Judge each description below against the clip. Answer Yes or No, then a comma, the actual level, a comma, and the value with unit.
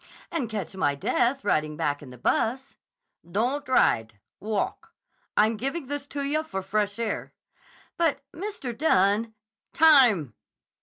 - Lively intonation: Yes, wide, 6.7 semitones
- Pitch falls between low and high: No, high, 225 Hz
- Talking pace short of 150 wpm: Yes, slow, 135 wpm